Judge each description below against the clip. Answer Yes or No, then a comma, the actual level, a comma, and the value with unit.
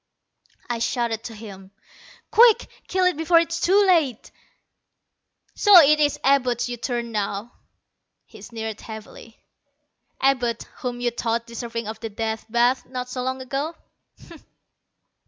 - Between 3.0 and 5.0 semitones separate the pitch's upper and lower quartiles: Yes, average, 3.7 semitones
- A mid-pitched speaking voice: No, high, 245 Hz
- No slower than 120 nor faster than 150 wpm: Yes, average, 140 wpm